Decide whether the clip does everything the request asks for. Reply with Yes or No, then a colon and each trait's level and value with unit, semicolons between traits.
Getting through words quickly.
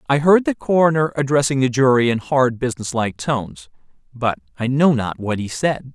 No: average, 190 wpm